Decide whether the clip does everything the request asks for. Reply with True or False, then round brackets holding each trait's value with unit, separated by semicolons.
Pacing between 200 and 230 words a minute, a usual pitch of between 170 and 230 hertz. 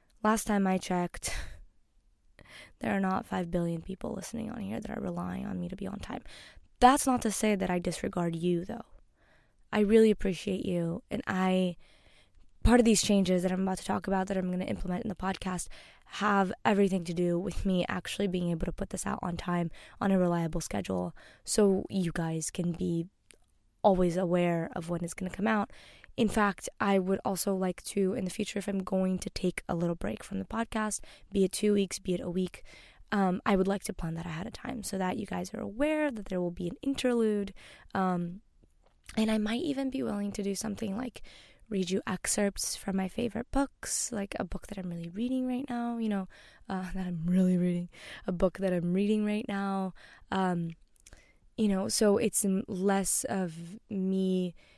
True (205 wpm; 190 Hz)